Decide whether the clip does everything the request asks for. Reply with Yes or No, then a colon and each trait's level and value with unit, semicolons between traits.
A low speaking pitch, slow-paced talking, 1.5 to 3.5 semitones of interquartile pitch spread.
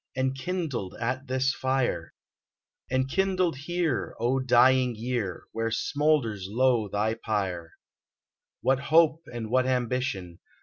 Yes: low, 130 Hz; slow, 115 wpm; average, 3.0 semitones